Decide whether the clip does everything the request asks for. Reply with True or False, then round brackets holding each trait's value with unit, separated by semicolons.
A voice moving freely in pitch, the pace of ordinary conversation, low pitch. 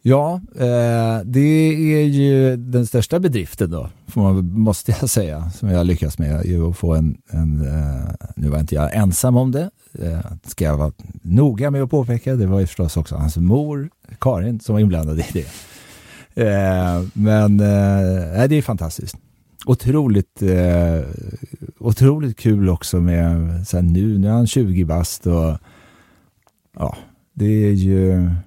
True (6.0 semitones; 160 wpm; 100 Hz)